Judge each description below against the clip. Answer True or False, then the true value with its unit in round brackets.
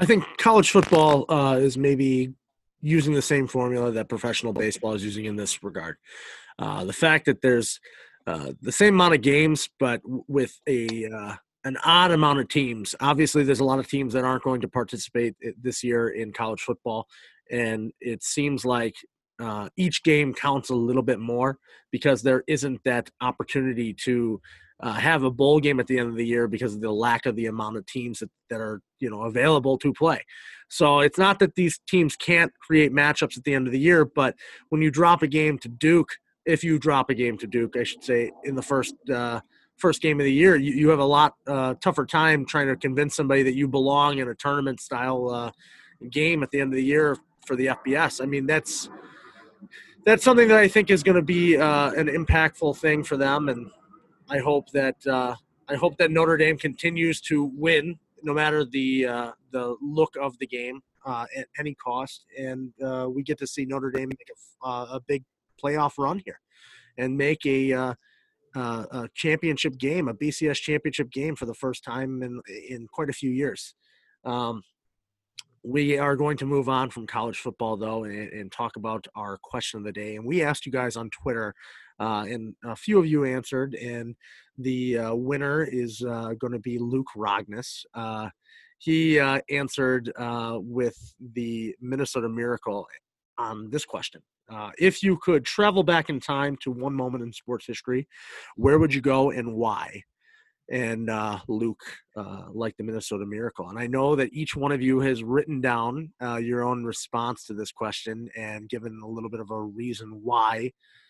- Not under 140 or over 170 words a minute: False (200 wpm)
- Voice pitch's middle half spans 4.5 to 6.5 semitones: False (3.9 semitones)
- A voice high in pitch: False (130 Hz)